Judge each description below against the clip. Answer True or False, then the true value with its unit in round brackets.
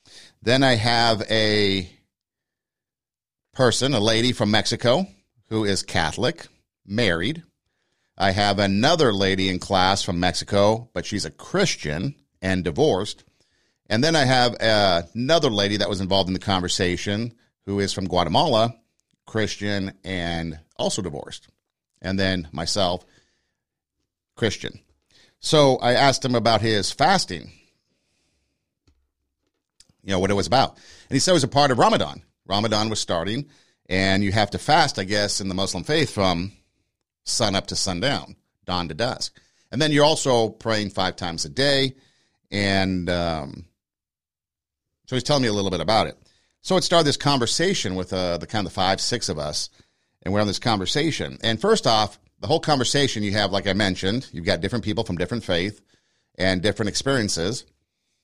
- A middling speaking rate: True (160 wpm)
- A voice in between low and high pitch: False (100 Hz)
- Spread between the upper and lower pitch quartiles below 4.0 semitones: False (4.3 semitones)